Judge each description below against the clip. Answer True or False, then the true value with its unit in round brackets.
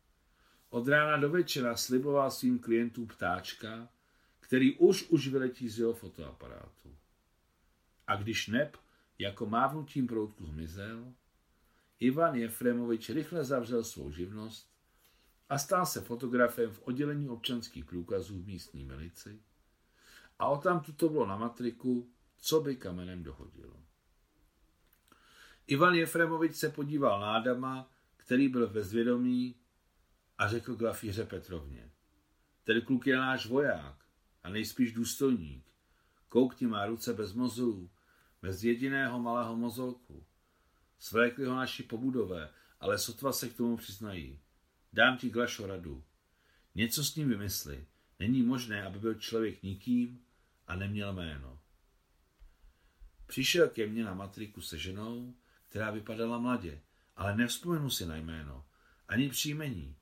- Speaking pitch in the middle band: False (115 Hz)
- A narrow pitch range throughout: False (7.1 semitones)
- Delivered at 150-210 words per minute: False (125 wpm)